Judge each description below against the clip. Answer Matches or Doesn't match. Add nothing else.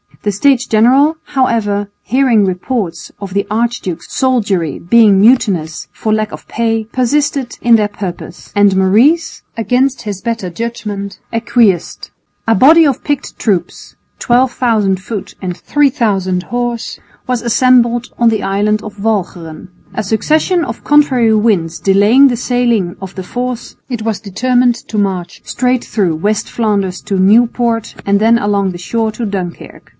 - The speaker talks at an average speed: Matches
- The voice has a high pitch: Matches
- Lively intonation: Doesn't match